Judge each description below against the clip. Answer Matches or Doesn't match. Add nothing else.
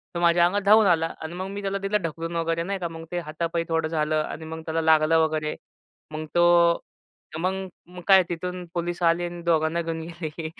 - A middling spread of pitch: Doesn't match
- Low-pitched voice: Doesn't match